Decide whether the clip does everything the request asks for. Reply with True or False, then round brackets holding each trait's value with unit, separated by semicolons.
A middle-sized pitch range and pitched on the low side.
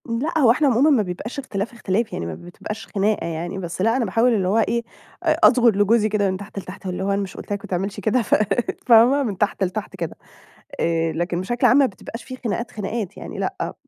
False (3.9 semitones; 210 Hz)